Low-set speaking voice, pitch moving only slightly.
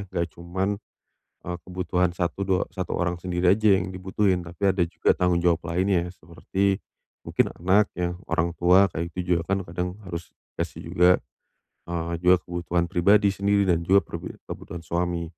Yes: very low, 90 Hz; narrow, 1.7 semitones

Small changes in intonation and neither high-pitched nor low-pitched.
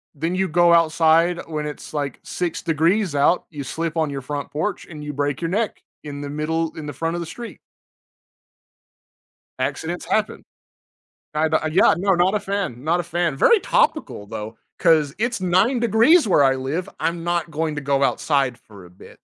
No: average, 3.6 semitones; medium, 160 Hz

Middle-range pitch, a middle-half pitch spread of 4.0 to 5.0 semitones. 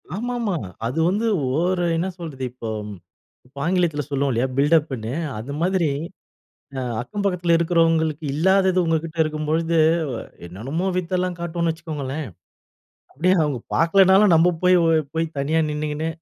No: medium, 165 Hz; average, 3.4 semitones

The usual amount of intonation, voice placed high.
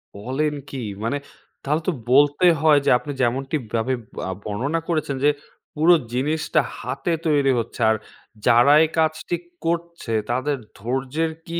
No: average, 3.7 semitones; medium, 145 Hz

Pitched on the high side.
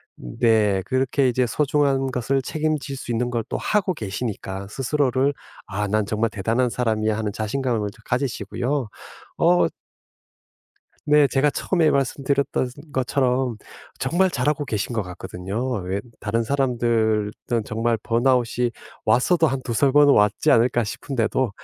No: low, 125 Hz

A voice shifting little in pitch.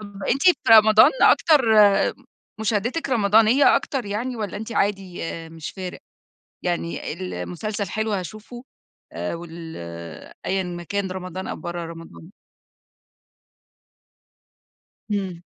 No: average, 3.6 semitones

